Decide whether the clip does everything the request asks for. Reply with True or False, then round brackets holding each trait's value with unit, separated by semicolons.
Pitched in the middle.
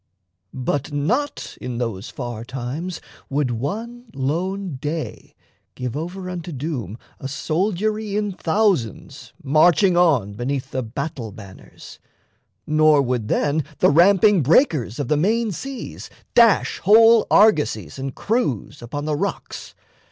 True (155 Hz)